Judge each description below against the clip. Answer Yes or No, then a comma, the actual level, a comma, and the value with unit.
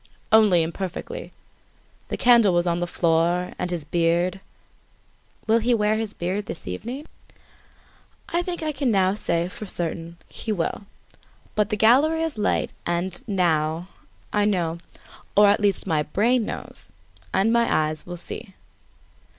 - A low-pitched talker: No, high, 190 Hz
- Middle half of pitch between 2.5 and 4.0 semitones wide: No, average, 4.4 semitones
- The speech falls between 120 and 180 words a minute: Yes, average, 150 wpm